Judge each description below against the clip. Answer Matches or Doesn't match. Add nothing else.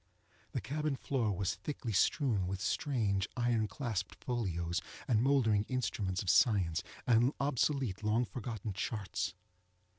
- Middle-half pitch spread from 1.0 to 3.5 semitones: Doesn't match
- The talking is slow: Matches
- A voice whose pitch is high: Doesn't match